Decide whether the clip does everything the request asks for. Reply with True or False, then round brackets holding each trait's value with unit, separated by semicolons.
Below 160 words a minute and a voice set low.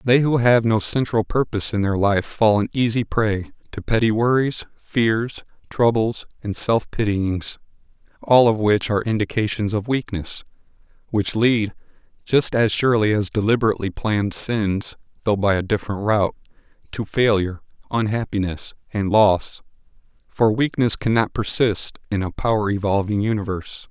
True (140 wpm; 110 Hz)